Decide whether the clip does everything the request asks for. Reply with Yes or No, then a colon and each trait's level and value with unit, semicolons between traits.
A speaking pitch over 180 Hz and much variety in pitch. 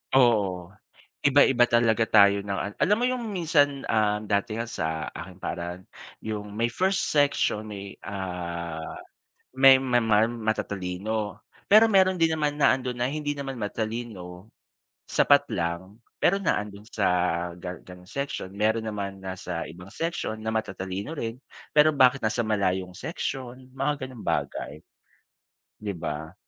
No: low, 110 Hz; wide, 5.9 semitones